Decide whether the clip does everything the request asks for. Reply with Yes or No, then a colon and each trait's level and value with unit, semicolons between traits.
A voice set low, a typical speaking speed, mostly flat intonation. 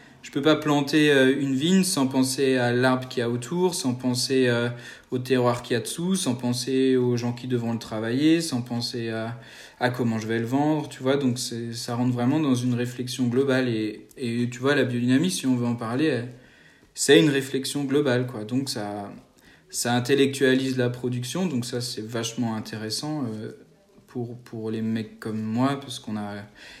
Yes: low, 125 Hz; average, 195 wpm; narrow, 2.2 semitones